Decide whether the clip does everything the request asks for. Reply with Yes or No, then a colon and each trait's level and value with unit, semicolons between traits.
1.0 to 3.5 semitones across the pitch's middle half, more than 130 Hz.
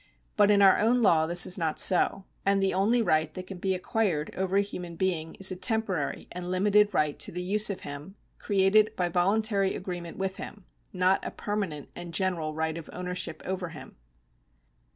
Yes: average, 2.7 semitones; medium, 185 Hz